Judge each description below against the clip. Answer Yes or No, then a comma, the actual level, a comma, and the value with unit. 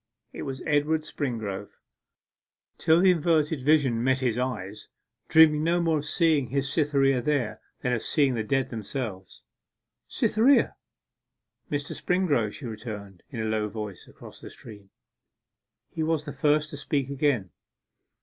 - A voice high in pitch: No, low, 135 Hz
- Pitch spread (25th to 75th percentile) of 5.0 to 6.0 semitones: Yes, wide, 5.4 semitones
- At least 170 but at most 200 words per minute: No, average, 145 wpm